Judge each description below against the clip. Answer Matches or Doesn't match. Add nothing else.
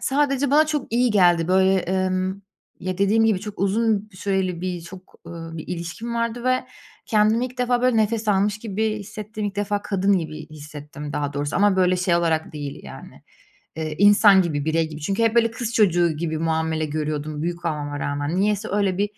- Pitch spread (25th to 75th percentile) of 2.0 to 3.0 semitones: Doesn't match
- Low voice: Doesn't match